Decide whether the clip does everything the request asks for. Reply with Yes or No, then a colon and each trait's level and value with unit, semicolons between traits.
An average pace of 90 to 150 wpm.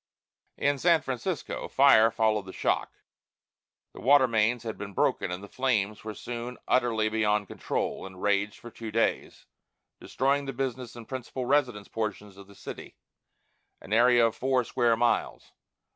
No: average, 160 wpm